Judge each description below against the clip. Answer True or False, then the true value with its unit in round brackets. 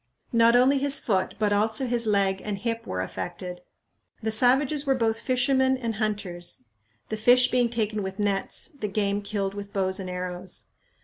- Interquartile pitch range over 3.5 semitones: True (3.9 semitones)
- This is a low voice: False (215 Hz)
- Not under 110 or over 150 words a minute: False (175 wpm)